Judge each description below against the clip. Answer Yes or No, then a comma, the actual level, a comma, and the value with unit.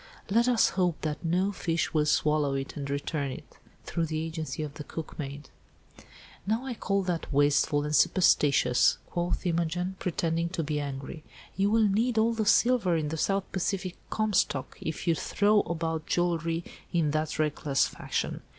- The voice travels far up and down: No, average, 4.1 semitones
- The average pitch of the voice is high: No, medium, 165 Hz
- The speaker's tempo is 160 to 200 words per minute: Yes, average, 165 wpm